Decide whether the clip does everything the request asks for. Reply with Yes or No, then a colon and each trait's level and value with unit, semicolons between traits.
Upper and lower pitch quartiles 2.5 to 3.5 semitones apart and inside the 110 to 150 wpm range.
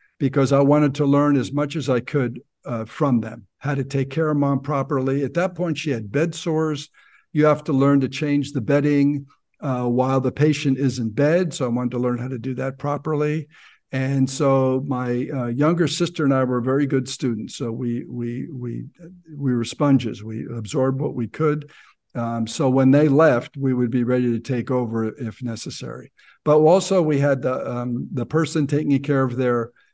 No: average, 2.9 semitones; fast, 205 wpm